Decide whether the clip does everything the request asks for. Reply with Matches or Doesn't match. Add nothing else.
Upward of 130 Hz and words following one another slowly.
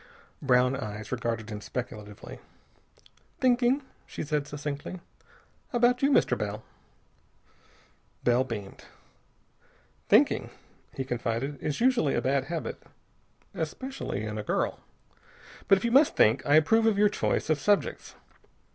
Matches